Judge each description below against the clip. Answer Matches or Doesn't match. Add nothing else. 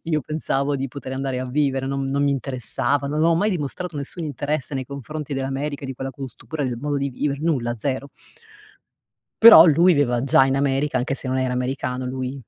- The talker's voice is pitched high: Doesn't match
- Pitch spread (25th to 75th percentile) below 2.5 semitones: Matches